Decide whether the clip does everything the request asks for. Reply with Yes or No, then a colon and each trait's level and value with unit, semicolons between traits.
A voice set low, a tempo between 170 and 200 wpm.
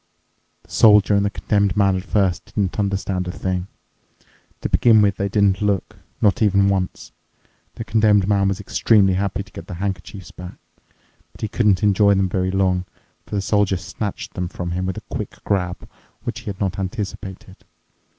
Yes: low, 100 Hz; average, 180 wpm